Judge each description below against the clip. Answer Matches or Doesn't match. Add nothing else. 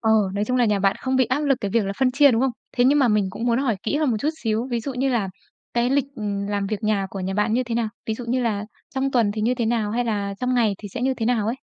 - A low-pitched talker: Doesn't match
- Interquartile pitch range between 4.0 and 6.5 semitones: Doesn't match